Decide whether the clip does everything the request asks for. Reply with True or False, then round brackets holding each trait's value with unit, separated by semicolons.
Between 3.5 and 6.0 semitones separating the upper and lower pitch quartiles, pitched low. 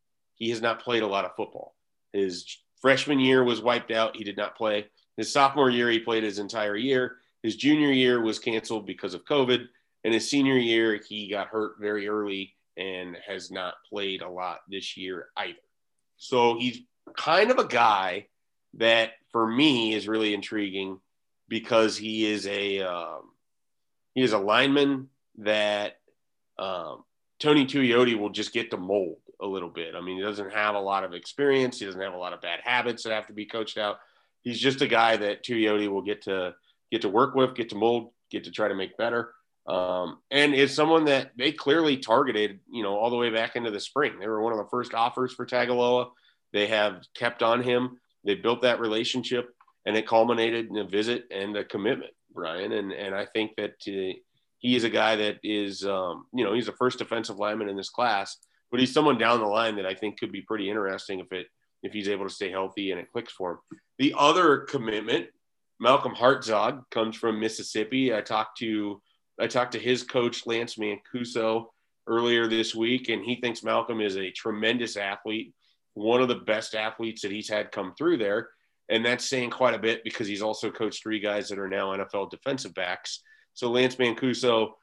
False (3.0 semitones; 110 Hz)